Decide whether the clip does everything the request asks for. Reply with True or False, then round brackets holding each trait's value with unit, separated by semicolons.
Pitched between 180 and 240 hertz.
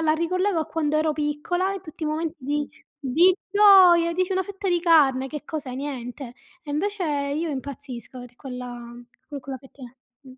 False (300 Hz)